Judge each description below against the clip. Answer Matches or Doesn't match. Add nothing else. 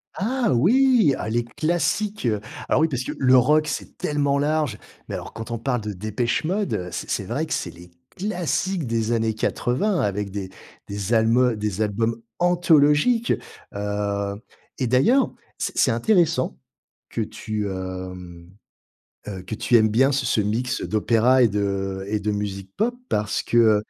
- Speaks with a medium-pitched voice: Doesn't match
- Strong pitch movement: Matches